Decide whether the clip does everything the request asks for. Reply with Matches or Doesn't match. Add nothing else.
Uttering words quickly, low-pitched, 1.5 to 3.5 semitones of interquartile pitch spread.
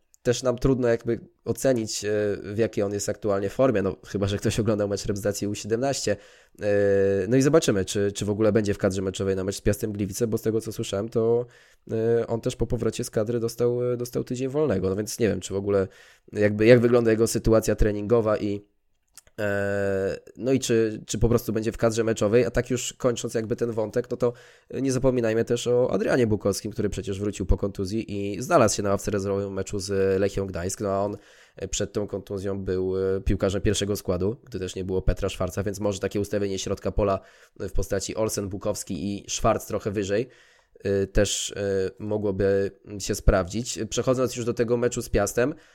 Matches